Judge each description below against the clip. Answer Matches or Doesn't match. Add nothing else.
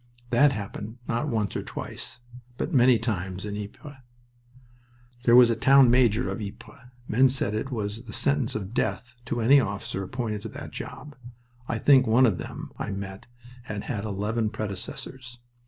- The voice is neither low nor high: Doesn't match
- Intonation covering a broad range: Doesn't match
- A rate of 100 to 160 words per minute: Doesn't match